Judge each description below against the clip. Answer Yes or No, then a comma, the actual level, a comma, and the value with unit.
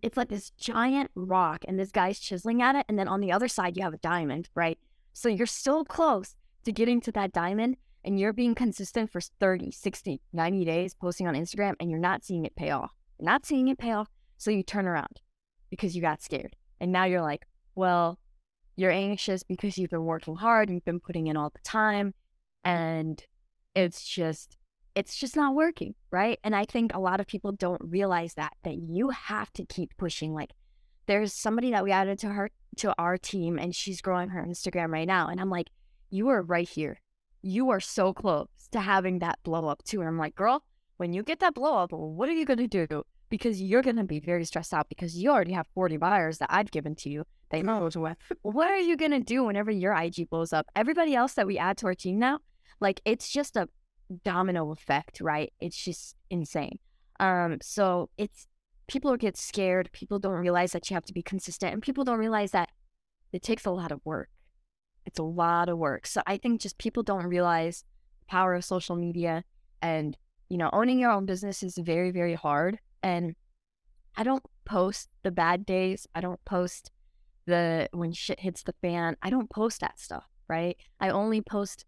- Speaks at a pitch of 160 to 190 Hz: Yes, medium, 185 Hz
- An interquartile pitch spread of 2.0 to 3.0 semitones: No, average, 3.9 semitones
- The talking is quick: Yes, fast, 210 wpm